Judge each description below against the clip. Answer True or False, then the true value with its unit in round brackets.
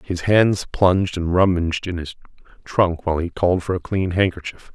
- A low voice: True (90 Hz)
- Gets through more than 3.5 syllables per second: True (5.4 syllables/s)